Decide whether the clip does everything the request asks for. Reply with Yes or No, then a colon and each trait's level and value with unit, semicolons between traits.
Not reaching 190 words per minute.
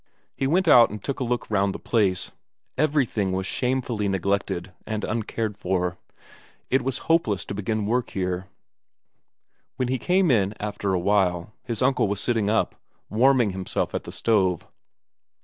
Yes: average, 160 wpm